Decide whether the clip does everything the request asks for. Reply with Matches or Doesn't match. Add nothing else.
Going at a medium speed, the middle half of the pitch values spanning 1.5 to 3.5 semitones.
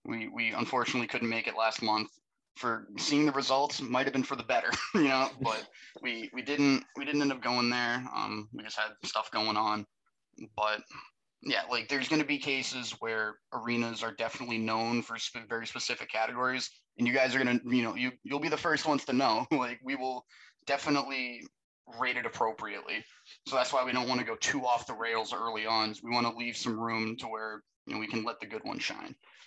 Doesn't match